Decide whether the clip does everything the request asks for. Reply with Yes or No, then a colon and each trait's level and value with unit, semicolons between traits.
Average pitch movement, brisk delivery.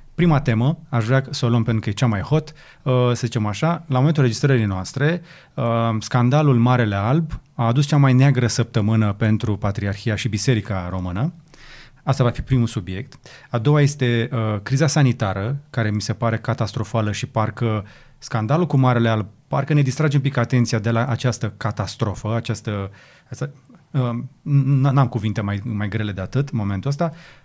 Yes: average, 3.9 semitones; fast, 175 wpm